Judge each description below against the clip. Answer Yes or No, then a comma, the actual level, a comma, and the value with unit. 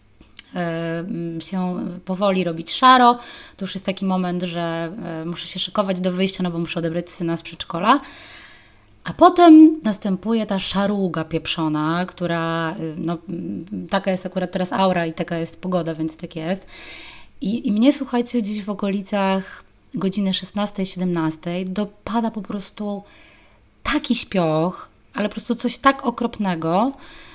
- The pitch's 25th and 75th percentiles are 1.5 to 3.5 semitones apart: No, average, 3.9 semitones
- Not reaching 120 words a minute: No, average, 135 wpm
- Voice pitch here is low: No, high, 190 Hz